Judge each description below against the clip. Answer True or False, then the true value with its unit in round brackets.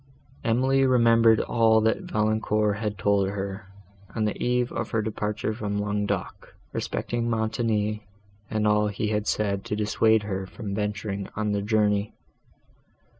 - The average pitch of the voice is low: True (105 Hz)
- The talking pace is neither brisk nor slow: True (145 wpm)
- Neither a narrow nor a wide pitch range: False (1.4 semitones)